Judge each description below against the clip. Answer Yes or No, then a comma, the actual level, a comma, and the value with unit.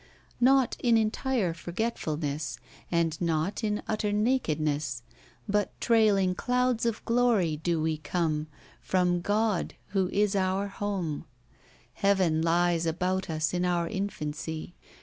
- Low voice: No, medium, 185 Hz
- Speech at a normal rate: No, slow, 125 wpm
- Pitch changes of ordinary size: Yes, average, 4.6 semitones